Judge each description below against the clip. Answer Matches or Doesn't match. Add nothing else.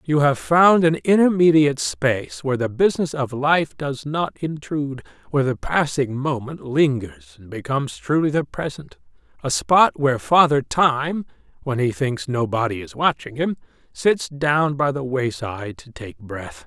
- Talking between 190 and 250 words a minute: Doesn't match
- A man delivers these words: Matches